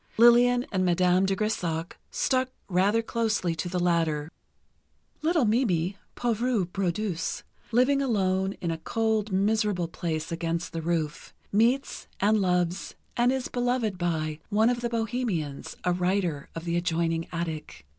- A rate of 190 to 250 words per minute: No, average, 140 wpm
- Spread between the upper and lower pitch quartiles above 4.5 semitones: Yes, average, 5.2 semitones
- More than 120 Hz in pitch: Yes, high, 190 Hz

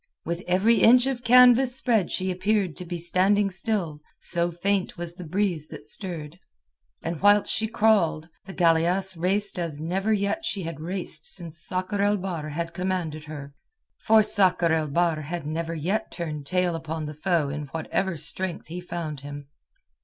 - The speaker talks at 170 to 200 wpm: Yes, average, 175 wpm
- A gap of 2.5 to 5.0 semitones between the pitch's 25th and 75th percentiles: Yes, average, 3.6 semitones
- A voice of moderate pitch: Yes, medium, 175 Hz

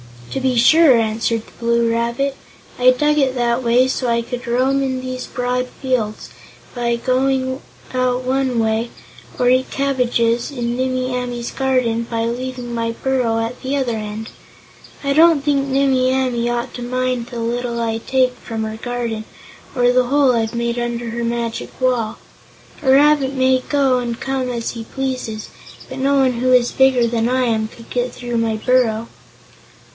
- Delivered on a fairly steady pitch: Yes, narrow, 1.9 semitones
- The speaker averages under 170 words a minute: No, average, 175 wpm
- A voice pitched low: No, high, 245 Hz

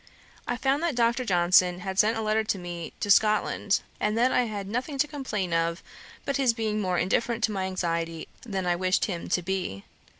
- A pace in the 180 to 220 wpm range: Yes, fast, 205 wpm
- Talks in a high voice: Yes, high, 205 Hz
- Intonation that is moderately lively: Yes, average, 4.5 semitones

